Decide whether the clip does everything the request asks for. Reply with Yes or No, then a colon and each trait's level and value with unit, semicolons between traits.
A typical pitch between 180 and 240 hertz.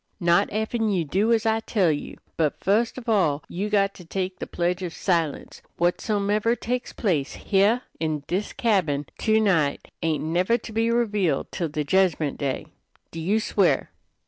Yes: high, 190 Hz